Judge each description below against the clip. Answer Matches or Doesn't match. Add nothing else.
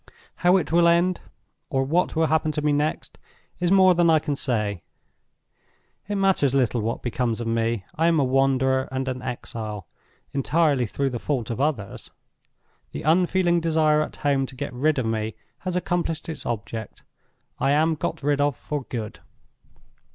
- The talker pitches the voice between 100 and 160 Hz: Matches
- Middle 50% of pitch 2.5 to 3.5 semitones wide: Doesn't match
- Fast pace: Doesn't match